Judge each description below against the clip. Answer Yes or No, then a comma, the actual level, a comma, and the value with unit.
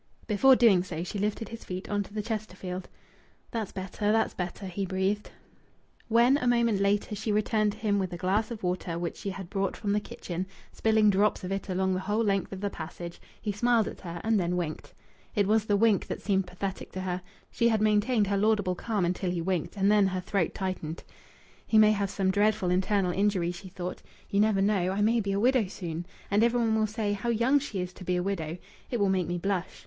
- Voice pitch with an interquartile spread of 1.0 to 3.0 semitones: Yes, narrow, 2.6 semitones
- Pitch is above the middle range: Yes, high, 200 Hz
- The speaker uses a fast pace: Yes, fast, 230 wpm